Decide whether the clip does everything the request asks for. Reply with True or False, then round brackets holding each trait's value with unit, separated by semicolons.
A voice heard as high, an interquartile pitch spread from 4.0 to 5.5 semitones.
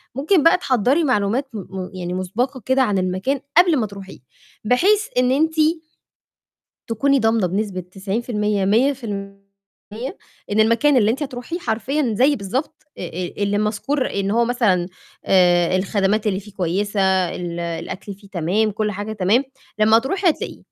True (215 Hz; 5.0 semitones)